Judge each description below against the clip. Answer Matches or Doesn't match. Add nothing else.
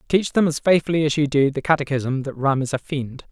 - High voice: Doesn't match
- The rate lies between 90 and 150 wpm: Doesn't match